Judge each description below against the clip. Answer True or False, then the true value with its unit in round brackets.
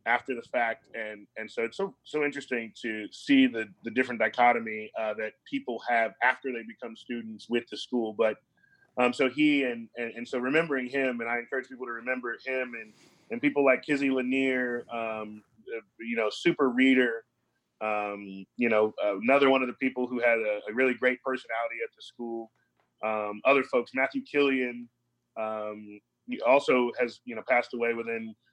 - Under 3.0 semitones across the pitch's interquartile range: True (2.5 semitones)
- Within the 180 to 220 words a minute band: True (185 wpm)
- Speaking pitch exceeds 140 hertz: False (120 Hz)